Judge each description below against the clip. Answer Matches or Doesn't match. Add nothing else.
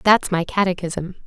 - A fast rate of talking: Doesn't match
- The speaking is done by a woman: Matches